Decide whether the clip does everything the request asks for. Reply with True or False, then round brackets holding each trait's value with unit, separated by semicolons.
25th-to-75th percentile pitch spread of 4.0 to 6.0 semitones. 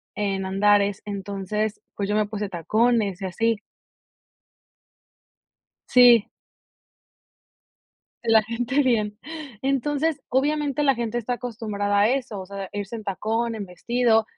False (3.2 semitones)